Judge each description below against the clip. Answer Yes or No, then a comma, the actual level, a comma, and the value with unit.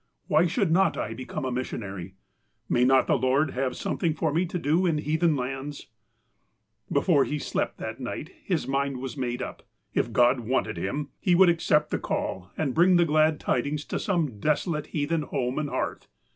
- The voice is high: No, medium, 145 Hz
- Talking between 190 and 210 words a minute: Yes, average, 195 wpm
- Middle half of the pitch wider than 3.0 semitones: Yes, average, 3.9 semitones